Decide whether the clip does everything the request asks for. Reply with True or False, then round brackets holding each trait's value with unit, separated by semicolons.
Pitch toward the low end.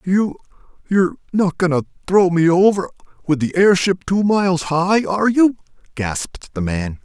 False (175 Hz)